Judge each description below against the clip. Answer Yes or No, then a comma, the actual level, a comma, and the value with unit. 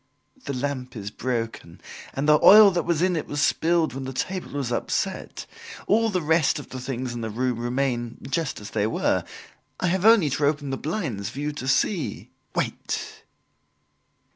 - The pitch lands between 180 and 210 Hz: No, medium, 140 Hz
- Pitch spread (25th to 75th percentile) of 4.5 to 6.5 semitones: Yes, average, 5.1 semitones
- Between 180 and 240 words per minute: Yes, average, 185 wpm